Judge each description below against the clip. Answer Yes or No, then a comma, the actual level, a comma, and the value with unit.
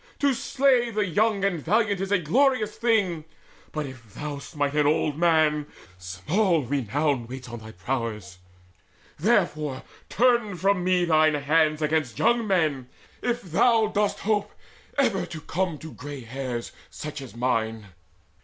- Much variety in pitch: Yes, wide, 6.9 semitones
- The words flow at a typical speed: Yes, average, 145 wpm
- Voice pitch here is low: No, medium, 155 Hz